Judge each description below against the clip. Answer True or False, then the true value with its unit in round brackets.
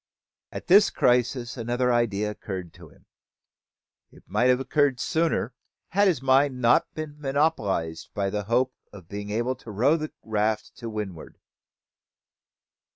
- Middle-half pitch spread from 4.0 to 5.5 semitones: True (4.6 semitones)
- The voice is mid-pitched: False (120 Hz)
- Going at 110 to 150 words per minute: True (145 wpm)